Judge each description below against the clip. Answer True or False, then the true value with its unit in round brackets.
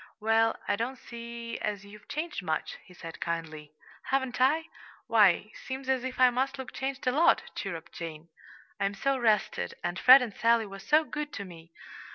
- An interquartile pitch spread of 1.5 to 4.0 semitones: False (5.1 semitones)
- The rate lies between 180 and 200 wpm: True (185 wpm)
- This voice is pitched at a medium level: False (230 Hz)